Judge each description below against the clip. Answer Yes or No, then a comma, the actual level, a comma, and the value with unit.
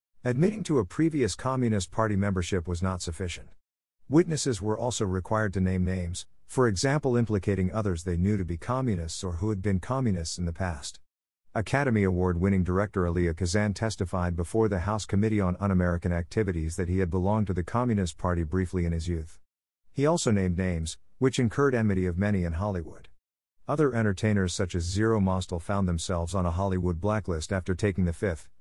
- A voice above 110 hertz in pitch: No, very low, 95 Hz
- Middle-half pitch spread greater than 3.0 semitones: Yes, average, 3.6 semitones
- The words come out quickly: No, average, 185 wpm